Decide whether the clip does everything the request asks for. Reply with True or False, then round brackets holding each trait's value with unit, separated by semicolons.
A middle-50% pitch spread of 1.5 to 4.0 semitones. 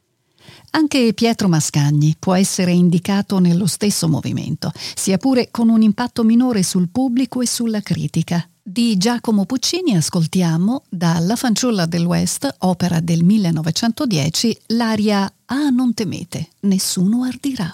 False (5.4 semitones)